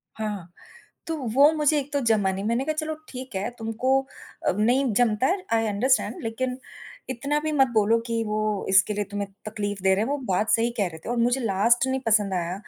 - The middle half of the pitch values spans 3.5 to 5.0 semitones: Yes, average, 4.3 semitones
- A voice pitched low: No, high, 225 Hz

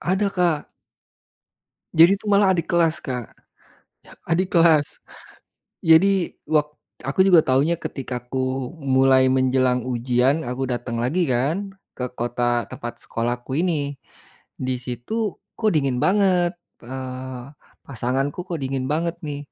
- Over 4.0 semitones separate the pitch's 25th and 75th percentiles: Yes, average, 5.1 semitones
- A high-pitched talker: No, low, 135 Hz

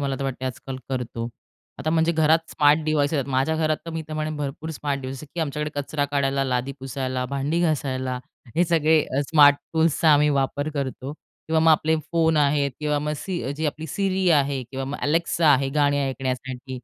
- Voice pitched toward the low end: No, medium, 145 Hz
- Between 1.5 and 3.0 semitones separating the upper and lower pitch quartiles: Yes, average, 2.7 semitones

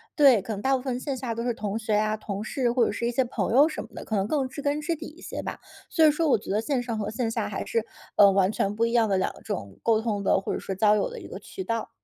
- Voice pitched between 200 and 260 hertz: Yes, high, 230 Hz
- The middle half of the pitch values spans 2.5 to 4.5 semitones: Yes, average, 4.2 semitones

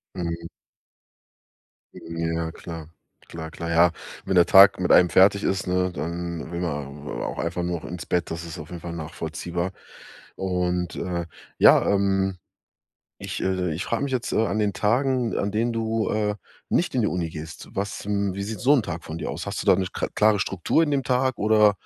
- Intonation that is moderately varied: Yes, average, 3.6 semitones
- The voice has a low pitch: Yes, very low, 90 Hz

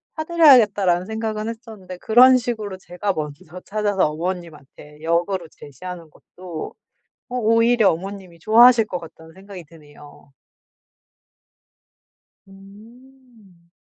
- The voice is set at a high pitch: Yes, high, 195 Hz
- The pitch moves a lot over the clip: No, average, 4.8 semitones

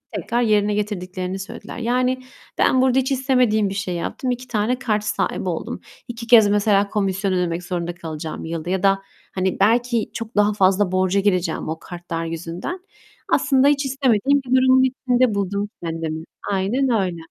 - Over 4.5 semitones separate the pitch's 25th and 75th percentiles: Yes, average, 5.2 semitones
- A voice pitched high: Yes, high, 205 Hz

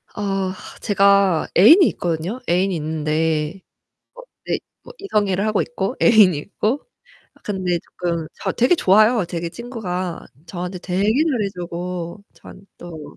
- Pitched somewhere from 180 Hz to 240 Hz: Yes, medium, 185 Hz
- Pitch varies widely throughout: No, average, 3.5 semitones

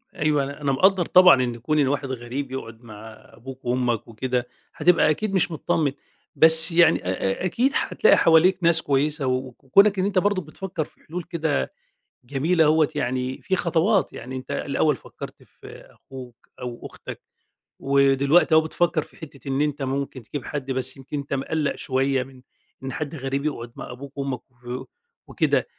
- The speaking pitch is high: No, medium, 140 Hz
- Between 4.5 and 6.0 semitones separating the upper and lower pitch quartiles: No, average, 3.8 semitones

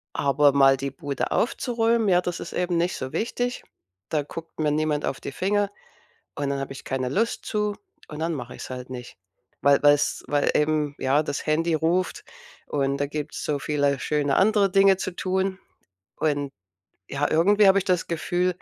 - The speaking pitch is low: No, medium, 155 Hz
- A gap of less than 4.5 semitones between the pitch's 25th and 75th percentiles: No, average, 4.8 semitones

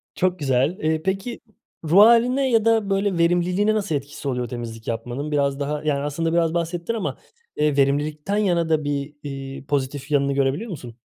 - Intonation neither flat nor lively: Yes, average, 5.0 semitones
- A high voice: No, medium, 155 Hz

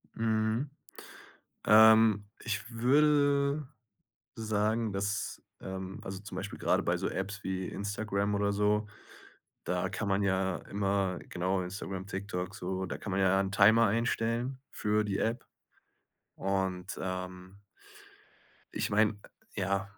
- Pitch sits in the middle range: No, low, 100 Hz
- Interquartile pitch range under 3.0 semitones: Yes, narrow, 2.5 semitones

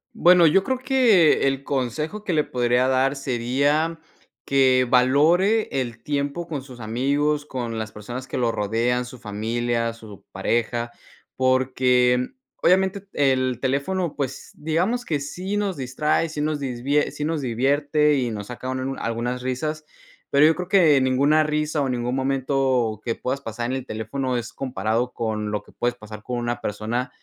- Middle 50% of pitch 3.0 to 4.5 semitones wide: Yes, average, 3.8 semitones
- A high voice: No, low, 130 Hz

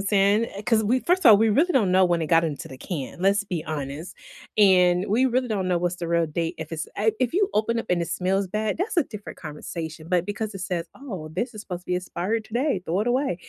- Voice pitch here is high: Yes, high, 195 Hz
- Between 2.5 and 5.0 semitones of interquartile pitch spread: Yes, average, 4.5 semitones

